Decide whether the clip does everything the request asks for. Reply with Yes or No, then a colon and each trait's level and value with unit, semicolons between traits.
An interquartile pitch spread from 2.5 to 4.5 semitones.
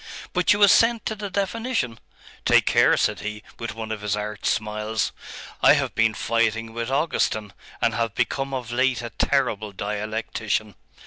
Yes: average, 4.1 semitones